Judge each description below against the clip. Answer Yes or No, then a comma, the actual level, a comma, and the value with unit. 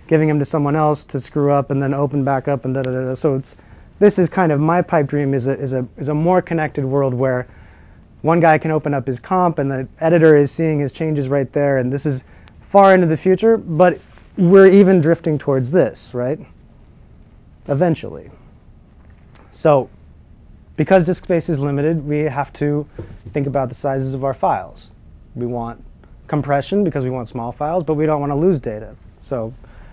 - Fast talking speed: No, average, 195 wpm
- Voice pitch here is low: No, medium, 145 Hz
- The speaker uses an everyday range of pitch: Yes, average, 3.6 semitones